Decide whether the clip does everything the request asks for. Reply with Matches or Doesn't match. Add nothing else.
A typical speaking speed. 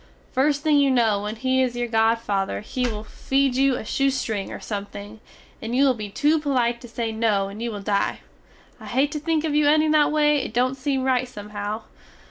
Doesn't match